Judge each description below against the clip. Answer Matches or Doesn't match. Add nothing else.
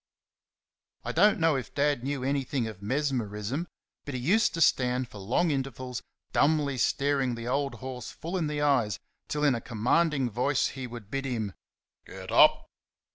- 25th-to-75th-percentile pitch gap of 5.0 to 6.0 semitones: Doesn't match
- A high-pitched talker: Doesn't match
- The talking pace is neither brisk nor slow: Matches